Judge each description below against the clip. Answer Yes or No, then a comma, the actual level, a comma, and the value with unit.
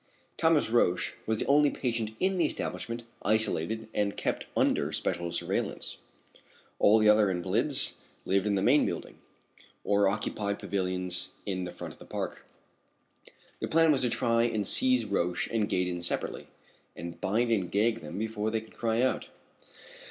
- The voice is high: No, low, 110 Hz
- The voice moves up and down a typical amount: Yes, average, 3.5 semitones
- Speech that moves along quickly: No, average, 160 wpm